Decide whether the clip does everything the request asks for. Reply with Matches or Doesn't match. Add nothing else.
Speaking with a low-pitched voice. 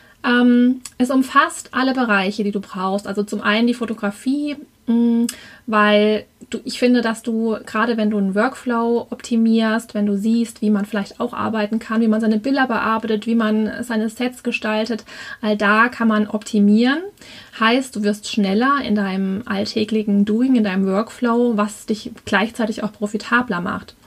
Doesn't match